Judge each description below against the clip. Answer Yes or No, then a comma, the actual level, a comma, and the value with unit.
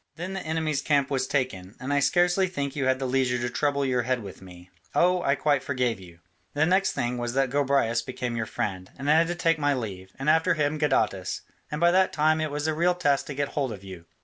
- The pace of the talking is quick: Yes, fast, 250 wpm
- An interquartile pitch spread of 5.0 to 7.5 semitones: No, average, 4.5 semitones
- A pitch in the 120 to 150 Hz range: Yes, medium, 140 Hz